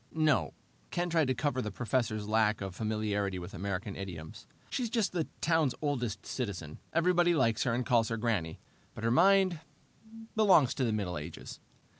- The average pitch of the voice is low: Yes, low, 115 Hz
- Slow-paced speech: No, average, 170 wpm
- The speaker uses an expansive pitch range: Yes, wide, 7.4 semitones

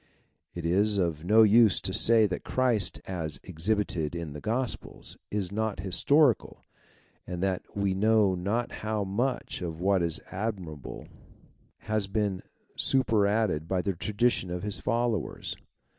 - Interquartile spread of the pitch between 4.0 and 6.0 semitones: No, average, 3.6 semitones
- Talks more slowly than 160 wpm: Yes, slow, 135 wpm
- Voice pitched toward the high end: No, low, 100 Hz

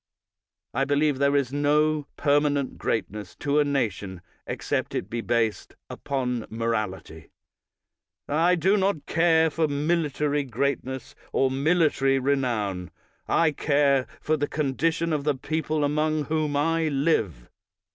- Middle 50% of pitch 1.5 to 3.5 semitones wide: Yes, average, 3.1 semitones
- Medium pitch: Yes, medium, 145 Hz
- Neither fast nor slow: No, slow, 125 wpm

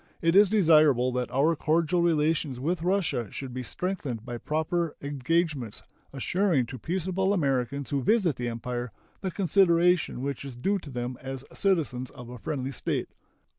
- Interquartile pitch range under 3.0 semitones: No, wide, 5.6 semitones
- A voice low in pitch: No, medium, 150 Hz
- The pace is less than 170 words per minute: Yes, average, 160 wpm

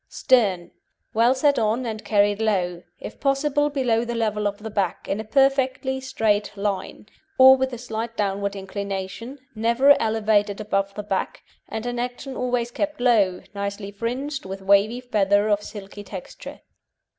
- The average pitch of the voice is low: No, high, 220 Hz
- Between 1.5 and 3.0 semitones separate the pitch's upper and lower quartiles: No, average, 3.7 semitones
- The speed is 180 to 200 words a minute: No, average, 155 wpm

